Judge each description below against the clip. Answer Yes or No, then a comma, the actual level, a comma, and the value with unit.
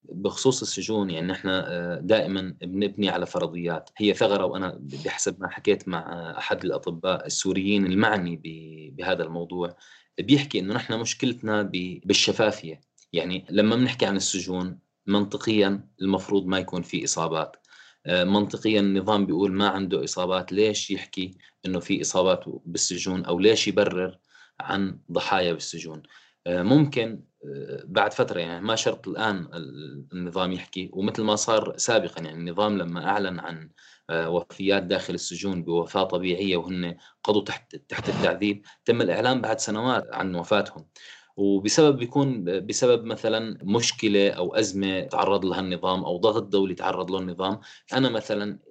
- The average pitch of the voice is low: Yes, very low, 95 Hz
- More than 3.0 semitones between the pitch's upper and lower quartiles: No, average, 2.7 semitones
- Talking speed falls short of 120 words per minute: No, average, 130 wpm